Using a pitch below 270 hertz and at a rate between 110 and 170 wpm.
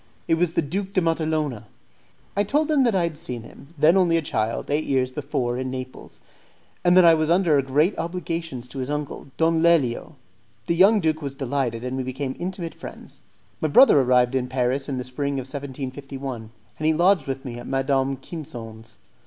No: medium, 140 Hz; average, 195 wpm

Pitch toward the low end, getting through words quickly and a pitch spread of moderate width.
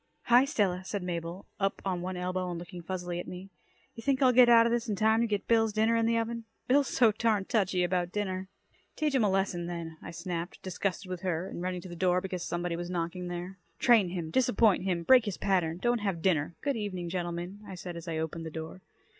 No: medium, 185 Hz; fast, 235 wpm; average, 3.9 semitones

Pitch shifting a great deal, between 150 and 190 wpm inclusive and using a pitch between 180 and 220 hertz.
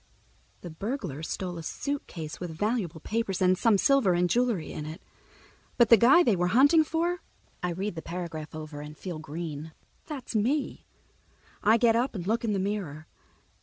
Yes: wide, 6.5 semitones; average, 170 wpm; high, 190 Hz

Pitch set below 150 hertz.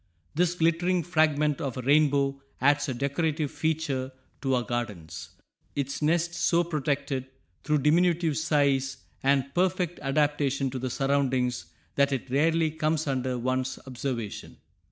Yes: medium, 140 Hz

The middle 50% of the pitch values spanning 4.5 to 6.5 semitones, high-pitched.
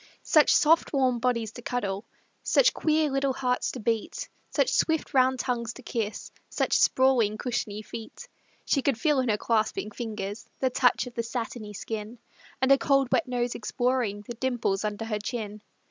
No: average, 3.3 semitones; high, 245 Hz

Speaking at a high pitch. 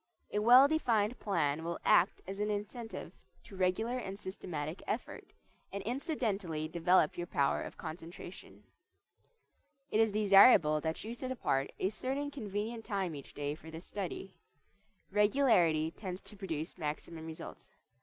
Yes: high, 195 Hz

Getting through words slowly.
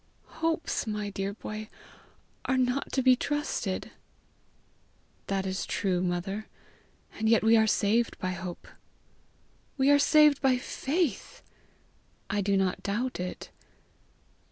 Yes: slow, 125 wpm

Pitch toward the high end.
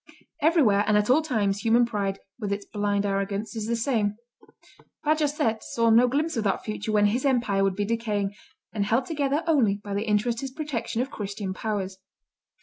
Yes: high, 220 Hz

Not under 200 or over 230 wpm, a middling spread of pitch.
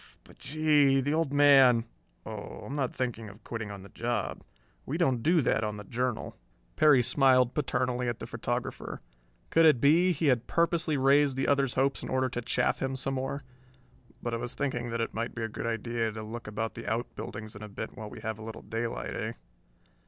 Yes: fast, 205 wpm; average, 3.6 semitones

